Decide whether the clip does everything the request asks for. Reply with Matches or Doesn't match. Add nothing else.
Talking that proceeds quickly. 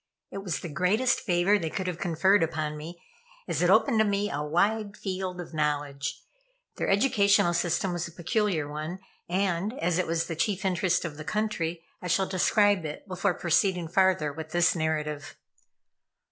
Doesn't match